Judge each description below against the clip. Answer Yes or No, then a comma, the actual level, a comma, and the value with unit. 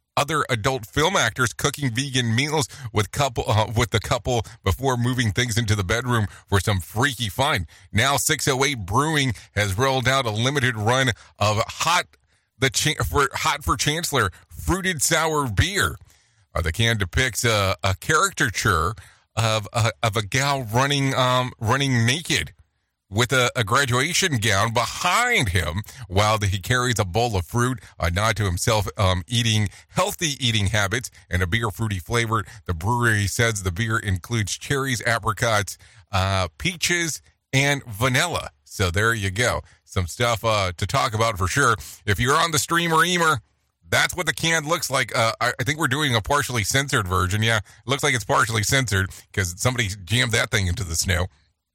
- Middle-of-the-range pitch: No, low, 115 Hz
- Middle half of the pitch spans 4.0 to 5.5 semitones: Yes, average, 4.6 semitones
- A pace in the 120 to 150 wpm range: No, average, 175 wpm